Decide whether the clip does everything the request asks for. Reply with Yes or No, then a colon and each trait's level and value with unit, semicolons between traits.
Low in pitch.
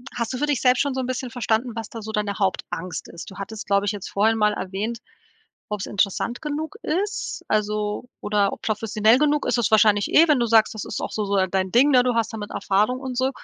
No: high, 220 Hz